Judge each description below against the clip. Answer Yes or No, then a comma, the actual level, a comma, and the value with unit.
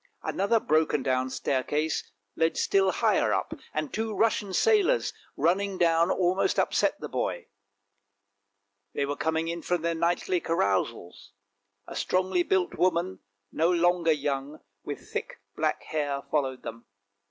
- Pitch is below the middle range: No, medium, 170 Hz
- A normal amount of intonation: Yes, average, 4.2 semitones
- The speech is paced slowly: Yes, slow, 130 wpm